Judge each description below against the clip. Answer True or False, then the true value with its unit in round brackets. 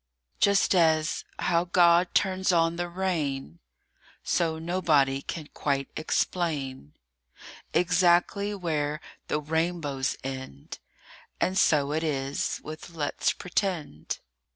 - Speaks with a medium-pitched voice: True (160 Hz)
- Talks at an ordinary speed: False (100 wpm)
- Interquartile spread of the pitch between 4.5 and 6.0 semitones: False (3.6 semitones)